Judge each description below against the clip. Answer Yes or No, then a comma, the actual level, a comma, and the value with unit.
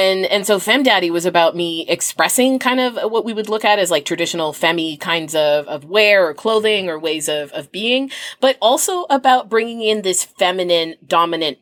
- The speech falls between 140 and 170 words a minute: No, average, 200 wpm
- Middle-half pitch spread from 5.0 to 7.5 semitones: Yes, average, 5.3 semitones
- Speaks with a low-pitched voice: No, medium, 185 Hz